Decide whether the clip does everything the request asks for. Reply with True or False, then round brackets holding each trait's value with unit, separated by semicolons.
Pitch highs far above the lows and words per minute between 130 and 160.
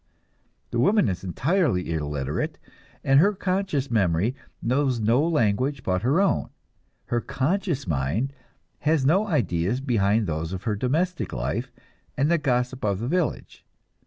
True (7.7 semitones; 140 wpm)